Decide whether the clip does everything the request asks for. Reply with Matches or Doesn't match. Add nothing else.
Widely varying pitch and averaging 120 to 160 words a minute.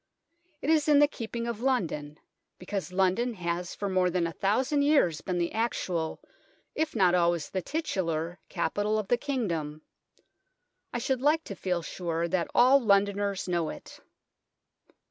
Matches